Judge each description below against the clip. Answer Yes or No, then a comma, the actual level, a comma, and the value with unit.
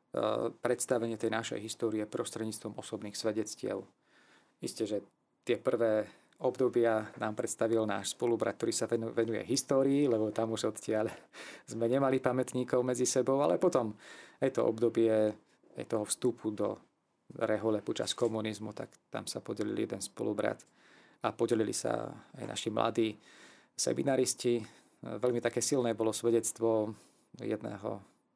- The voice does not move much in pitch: Yes, narrow, 2.1 semitones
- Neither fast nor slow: Yes, average, 125 wpm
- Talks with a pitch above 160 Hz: No, low, 115 Hz